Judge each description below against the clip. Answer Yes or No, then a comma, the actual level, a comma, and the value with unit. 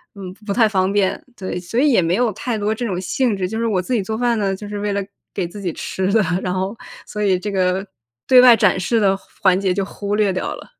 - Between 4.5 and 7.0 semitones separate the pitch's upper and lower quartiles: No, average, 2.8 semitones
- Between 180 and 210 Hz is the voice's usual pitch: Yes, high, 200 Hz